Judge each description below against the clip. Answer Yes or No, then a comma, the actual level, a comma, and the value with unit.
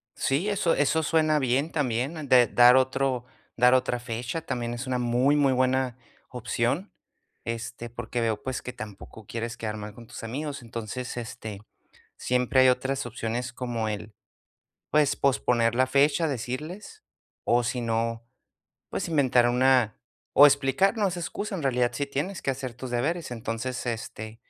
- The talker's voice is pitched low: Yes, low, 125 Hz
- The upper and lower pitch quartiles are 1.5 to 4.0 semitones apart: Yes, average, 3.0 semitones